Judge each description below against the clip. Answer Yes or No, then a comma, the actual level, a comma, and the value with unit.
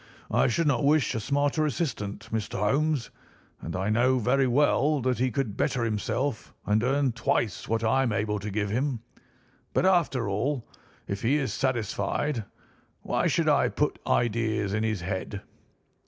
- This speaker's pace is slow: No, average, 165 wpm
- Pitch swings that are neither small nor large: Yes, average, 4.5 semitones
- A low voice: Yes, low, 120 Hz